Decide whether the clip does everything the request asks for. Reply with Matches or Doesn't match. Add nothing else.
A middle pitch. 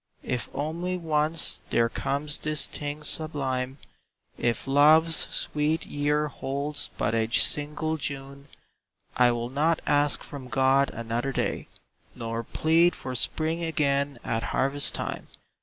Matches